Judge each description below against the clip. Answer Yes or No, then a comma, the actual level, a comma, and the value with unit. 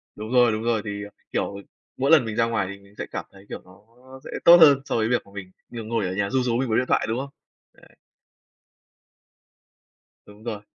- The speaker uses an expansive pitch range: No, average, 3.4 semitones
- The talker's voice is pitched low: Yes, low, 115 Hz